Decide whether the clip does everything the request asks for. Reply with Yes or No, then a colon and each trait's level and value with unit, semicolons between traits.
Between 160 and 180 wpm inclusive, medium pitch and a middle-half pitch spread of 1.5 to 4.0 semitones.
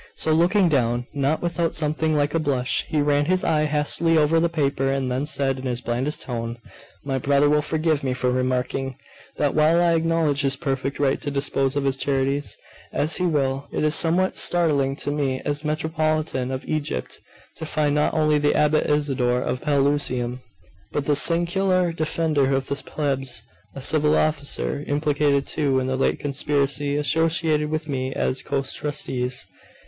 Yes: average, 175 wpm; medium, 145 Hz; narrow, 2.5 semitones